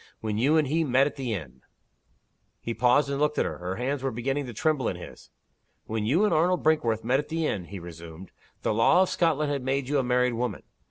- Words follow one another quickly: Yes, fast, 240 wpm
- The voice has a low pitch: Yes, low, 130 Hz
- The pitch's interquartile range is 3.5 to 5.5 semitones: Yes, average, 5.0 semitones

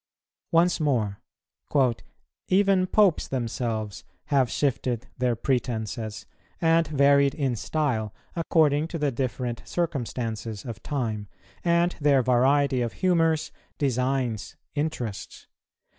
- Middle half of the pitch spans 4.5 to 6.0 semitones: Yes, average, 5.0 semitones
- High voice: No, low, 135 Hz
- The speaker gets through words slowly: Yes, slow, 100 wpm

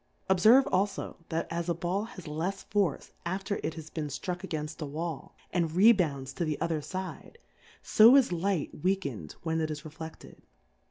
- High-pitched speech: No, medium, 170 Hz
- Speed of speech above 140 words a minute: Yes, average, 170 wpm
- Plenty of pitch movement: No, average, 3.6 semitones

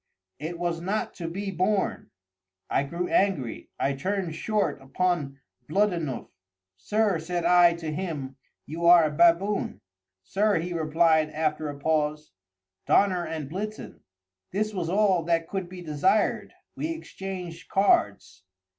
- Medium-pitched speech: Yes, medium, 170 Hz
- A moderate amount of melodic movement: Yes, average, 3.8 semitones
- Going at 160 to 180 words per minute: No, slow, 135 wpm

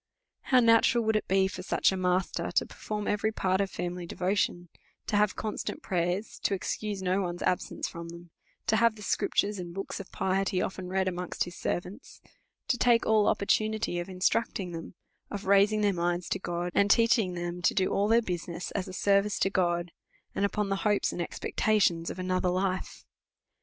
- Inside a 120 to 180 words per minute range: No, average, 190 wpm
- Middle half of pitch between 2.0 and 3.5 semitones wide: Yes, average, 2.7 semitones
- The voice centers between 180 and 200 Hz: Yes, high, 190 Hz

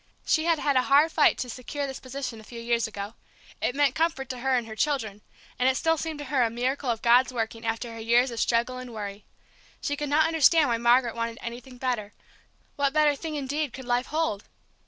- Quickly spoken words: Yes, fast, 225 wpm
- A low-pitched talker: No, very high, 255 Hz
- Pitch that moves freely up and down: No, average, 3.7 semitones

